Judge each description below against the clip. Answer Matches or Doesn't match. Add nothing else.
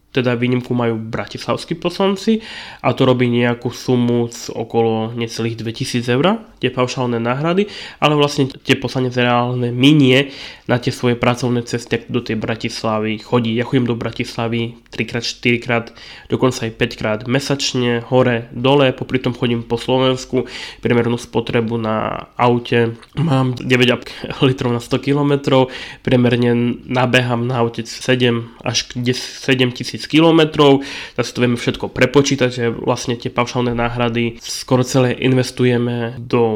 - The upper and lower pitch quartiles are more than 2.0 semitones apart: Doesn't match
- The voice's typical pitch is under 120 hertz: Doesn't match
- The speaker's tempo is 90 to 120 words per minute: Doesn't match